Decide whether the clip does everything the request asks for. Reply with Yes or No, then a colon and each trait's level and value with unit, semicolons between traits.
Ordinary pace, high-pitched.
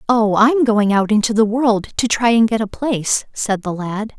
No: fast, 230 wpm; high, 220 Hz